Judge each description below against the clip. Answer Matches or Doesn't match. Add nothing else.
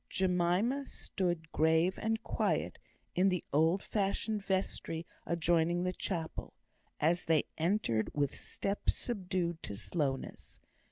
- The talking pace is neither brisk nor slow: Doesn't match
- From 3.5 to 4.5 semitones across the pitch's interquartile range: Doesn't match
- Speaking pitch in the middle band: Matches